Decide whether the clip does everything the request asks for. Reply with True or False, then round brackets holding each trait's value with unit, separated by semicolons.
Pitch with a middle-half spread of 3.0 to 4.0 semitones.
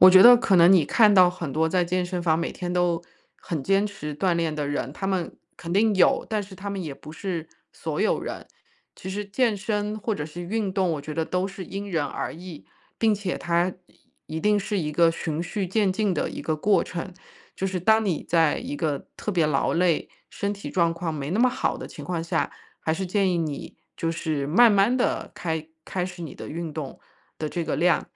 True (3.6 semitones)